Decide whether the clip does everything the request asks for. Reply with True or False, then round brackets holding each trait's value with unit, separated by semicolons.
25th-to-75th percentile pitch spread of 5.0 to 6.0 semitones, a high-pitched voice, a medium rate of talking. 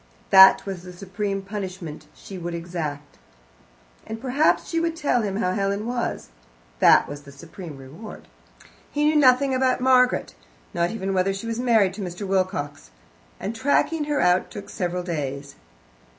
True (5.6 semitones; 195 Hz; 160 wpm)